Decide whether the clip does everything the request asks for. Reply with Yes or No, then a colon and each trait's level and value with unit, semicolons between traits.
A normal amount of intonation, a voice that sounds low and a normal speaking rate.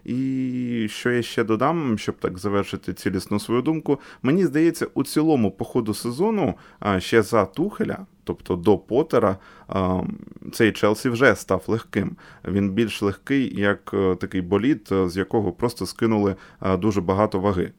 Yes: average, 3.8 semitones; low, 105 Hz; average, 140 wpm